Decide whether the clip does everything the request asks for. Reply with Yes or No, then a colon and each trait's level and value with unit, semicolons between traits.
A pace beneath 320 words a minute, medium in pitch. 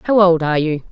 Yes: fast, 260 wpm; medium, 170 Hz